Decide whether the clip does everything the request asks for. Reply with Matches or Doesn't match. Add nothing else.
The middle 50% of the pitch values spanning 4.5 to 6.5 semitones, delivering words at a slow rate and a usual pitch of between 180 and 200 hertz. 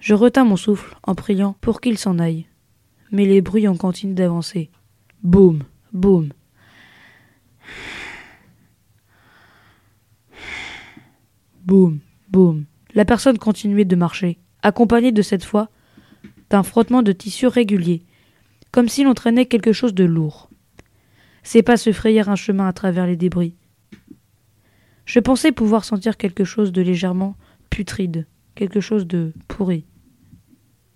Matches